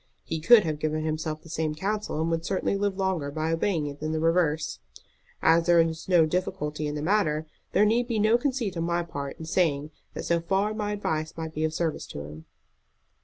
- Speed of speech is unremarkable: No, fast, 220 wpm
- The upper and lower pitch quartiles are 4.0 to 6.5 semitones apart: No, average, 3.6 semitones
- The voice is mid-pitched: Yes, medium, 165 Hz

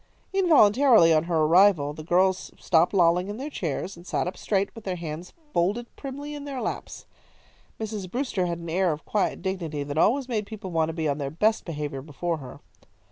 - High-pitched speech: No, medium, 180 Hz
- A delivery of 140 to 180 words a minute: No, average, 200 wpm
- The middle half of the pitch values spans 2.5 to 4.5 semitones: No, average, 5.1 semitones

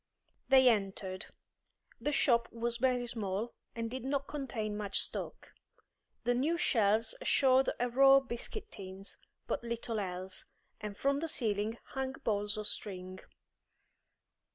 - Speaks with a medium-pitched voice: No, high, 235 Hz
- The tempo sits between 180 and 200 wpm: No, slow, 135 wpm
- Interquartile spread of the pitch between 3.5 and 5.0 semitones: Yes, average, 4.3 semitones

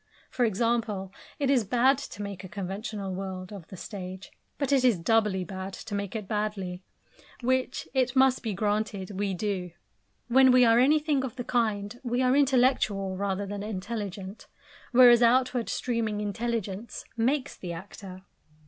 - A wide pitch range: No, average, 4.2 semitones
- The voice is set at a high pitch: Yes, high, 215 Hz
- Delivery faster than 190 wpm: No, average, 155 wpm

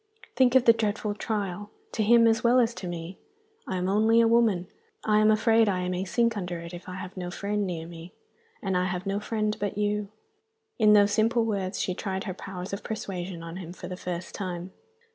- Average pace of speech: No, fast, 220 wpm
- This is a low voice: No, high, 200 Hz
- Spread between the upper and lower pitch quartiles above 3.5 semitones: No, average, 3.1 semitones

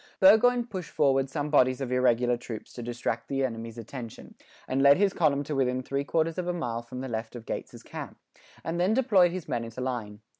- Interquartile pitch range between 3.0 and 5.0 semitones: No, wide, 5.6 semitones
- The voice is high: No, low, 135 Hz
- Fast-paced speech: Yes, fast, 220 wpm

